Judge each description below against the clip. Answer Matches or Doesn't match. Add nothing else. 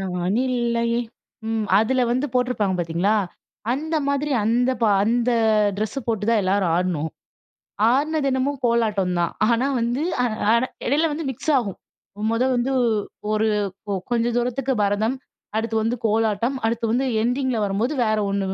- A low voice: Doesn't match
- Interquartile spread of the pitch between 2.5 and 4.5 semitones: Matches